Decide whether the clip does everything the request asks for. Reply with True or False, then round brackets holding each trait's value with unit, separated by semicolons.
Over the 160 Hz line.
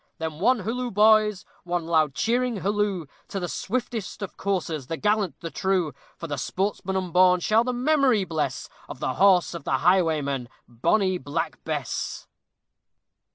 True (185 Hz)